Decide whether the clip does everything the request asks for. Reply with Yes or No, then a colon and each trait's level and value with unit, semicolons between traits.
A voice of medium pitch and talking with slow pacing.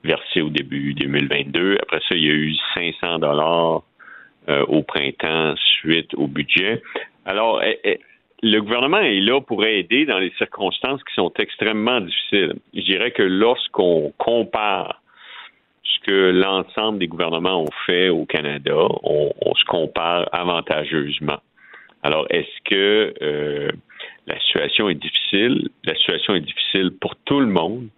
No: very low, 85 Hz; slow, 140 wpm